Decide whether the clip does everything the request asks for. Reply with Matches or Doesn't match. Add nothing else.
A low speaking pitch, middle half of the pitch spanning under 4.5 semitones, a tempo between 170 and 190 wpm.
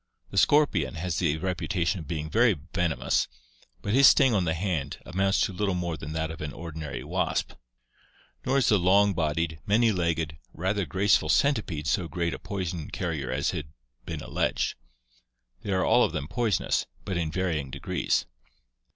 Matches